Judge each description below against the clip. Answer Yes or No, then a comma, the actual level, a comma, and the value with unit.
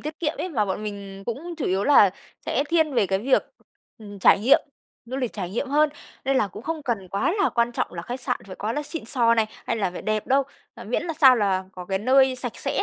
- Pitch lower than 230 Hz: No, high, 235 Hz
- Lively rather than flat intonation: Yes, wide, 5.7 semitones